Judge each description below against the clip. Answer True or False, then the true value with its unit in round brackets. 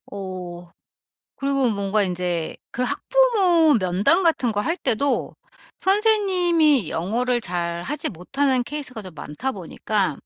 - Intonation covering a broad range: True (8.7 semitones)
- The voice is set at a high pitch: True (245 Hz)